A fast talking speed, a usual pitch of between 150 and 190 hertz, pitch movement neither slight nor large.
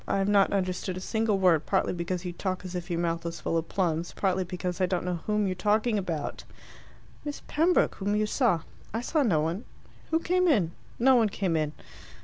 Yes: fast, 215 wpm; medium, 185 Hz; average, 3.5 semitones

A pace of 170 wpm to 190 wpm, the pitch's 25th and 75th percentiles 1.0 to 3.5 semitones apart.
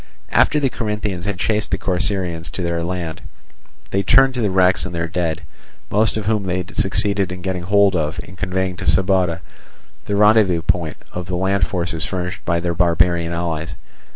Yes: average, 180 wpm; average, 2.7 semitones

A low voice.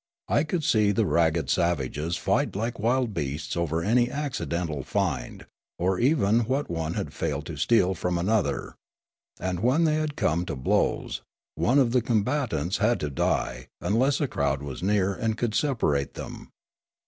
Yes: low, 100 Hz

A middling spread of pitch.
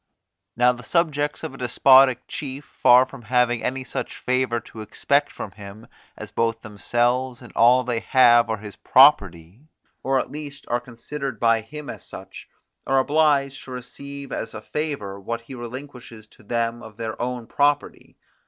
Yes: average, 3.1 semitones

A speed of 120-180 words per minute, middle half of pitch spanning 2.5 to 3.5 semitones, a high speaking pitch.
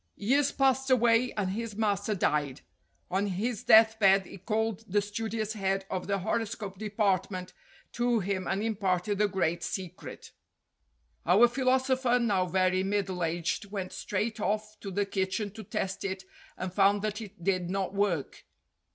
Yes: average, 155 wpm; average, 2.8 semitones; high, 200 Hz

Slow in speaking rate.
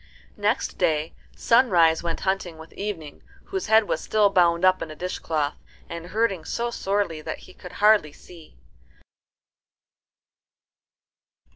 Yes: slow, 130 wpm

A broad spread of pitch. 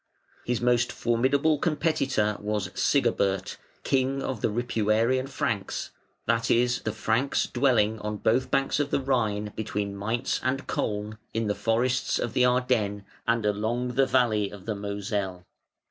No: average, 3.6 semitones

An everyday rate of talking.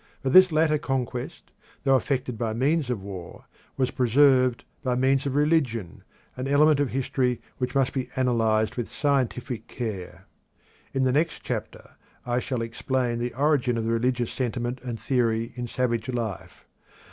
Yes: average, 160 wpm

